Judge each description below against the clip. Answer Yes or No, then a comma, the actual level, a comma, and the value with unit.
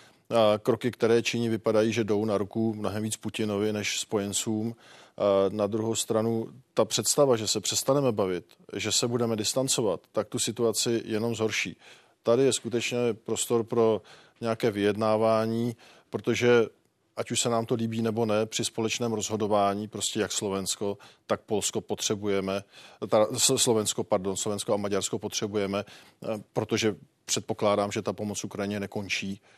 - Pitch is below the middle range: Yes, low, 110 Hz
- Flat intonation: Yes, narrow, 2.0 semitones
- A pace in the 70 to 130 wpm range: No, average, 145 wpm